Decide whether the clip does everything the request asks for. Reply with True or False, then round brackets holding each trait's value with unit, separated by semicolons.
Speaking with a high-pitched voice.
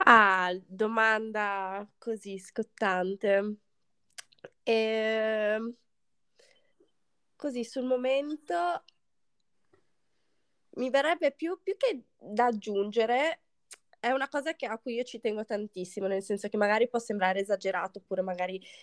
True (220 Hz)